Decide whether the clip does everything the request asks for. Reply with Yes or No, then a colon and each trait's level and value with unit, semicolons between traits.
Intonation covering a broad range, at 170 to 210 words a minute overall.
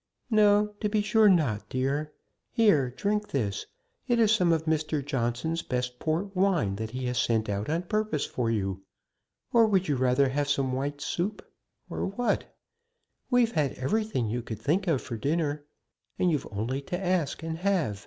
Yes: wide, 7.6 semitones; average, 175 wpm